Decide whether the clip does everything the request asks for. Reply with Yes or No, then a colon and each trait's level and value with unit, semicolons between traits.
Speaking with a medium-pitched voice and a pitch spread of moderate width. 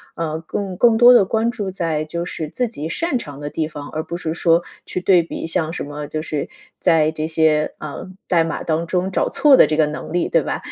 Yes: medium, 165 Hz; average, 3.2 semitones